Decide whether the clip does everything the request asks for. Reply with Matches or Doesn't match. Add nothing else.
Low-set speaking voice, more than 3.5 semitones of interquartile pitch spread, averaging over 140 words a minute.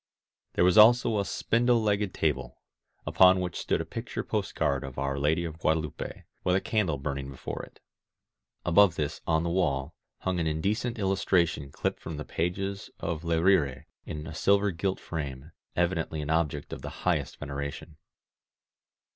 Matches